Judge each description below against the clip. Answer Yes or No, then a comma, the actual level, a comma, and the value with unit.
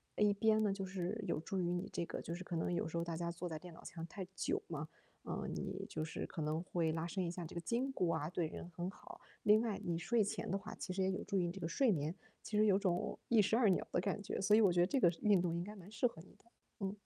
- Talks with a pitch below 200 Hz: Yes, medium, 185 Hz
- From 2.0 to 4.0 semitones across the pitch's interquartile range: Yes, average, 3.4 semitones